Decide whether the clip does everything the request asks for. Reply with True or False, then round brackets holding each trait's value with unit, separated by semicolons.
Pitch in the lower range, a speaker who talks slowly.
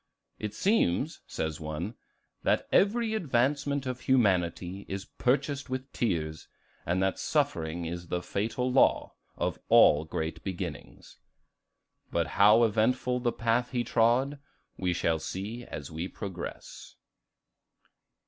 True (105 Hz; 120 wpm)